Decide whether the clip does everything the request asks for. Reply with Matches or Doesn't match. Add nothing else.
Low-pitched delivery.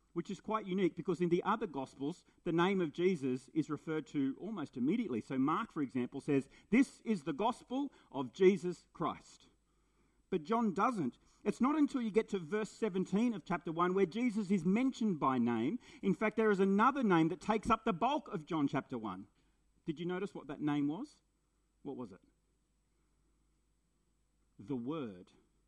Doesn't match